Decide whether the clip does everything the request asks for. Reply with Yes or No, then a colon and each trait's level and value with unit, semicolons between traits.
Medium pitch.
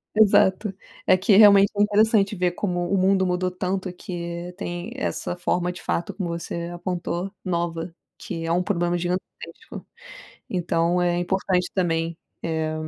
Yes: medium, 180 Hz